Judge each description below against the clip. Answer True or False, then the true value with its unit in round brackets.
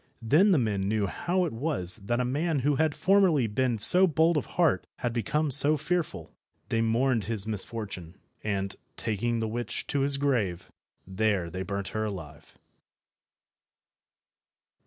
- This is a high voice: False (120 Hz)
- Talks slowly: False (155 wpm)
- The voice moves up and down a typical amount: False (6.4 semitones)